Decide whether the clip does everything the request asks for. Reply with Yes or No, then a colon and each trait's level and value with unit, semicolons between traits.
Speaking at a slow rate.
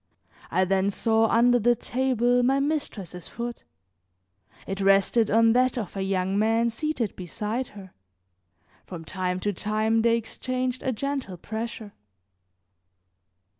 Yes: slow, 130 wpm